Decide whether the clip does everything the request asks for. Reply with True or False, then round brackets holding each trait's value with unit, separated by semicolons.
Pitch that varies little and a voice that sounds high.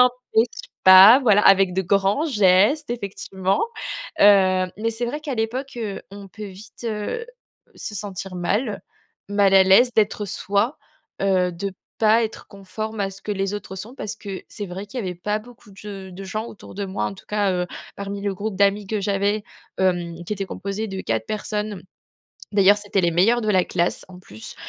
True (2.2 semitones; 200 Hz)